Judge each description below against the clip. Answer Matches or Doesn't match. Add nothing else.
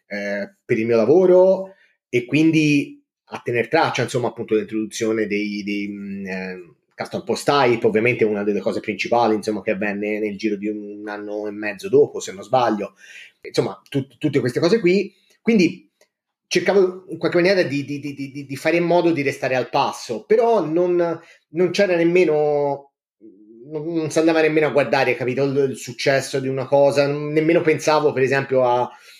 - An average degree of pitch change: Doesn't match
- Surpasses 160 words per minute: Matches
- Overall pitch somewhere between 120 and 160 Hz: Matches